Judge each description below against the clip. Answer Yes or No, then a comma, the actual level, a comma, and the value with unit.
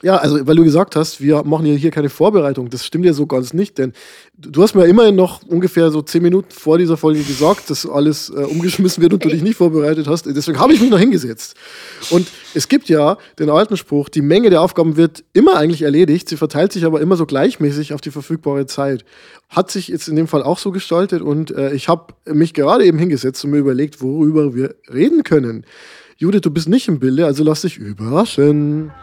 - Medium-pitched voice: Yes, medium, 160 Hz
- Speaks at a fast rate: Yes, fast, 225 wpm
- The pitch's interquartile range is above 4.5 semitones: No, average, 3.2 semitones